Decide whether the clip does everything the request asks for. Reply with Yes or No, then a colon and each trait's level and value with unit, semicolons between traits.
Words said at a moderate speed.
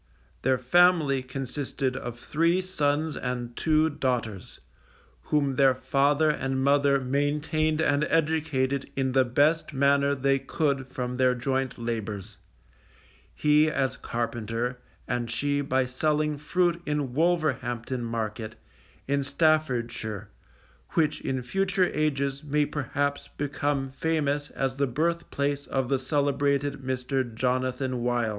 No: slow, 125 wpm